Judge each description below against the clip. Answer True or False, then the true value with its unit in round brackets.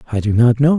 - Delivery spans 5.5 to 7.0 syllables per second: True (6.7 syllables/s)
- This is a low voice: True (125 Hz)